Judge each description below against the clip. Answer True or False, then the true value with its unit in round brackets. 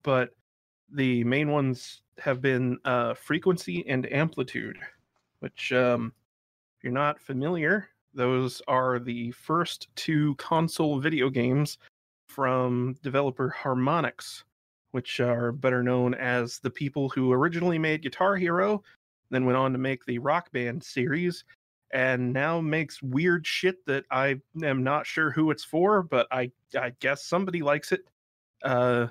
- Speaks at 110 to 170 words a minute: True (140 wpm)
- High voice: False (135 Hz)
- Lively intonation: False (3.8 semitones)